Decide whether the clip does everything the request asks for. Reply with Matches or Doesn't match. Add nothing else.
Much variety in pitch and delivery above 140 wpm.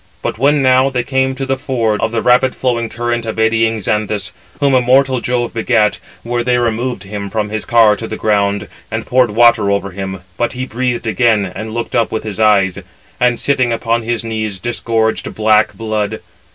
Doesn't match